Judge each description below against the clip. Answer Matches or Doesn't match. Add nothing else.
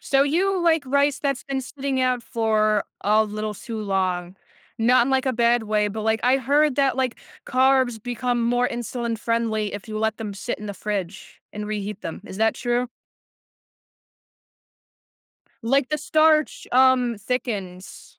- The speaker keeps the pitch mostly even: Doesn't match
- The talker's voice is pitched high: Matches